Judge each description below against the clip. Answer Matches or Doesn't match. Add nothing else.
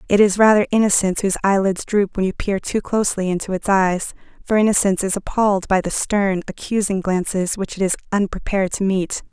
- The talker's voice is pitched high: Matches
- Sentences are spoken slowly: Doesn't match